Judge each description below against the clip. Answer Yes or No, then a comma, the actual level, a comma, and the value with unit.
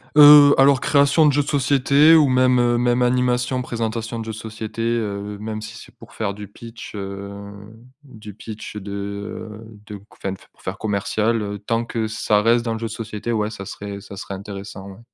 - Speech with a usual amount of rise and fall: Yes, average, 3.1 semitones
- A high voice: No, low, 110 Hz